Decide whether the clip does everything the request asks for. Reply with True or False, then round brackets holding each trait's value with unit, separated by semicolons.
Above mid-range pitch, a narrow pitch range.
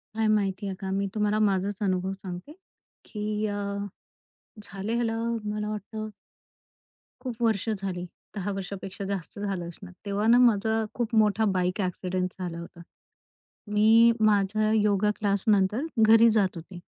True (205 Hz; 2.2 semitones)